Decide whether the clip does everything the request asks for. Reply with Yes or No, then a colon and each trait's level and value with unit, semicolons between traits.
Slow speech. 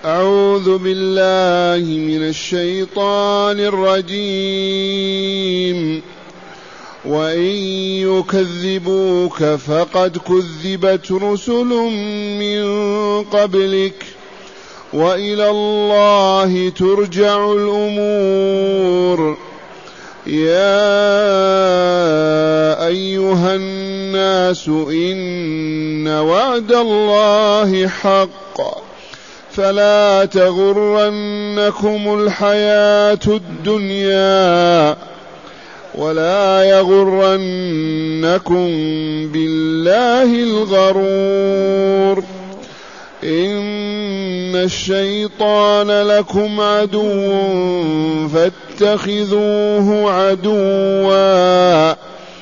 Yes: slow, 40 wpm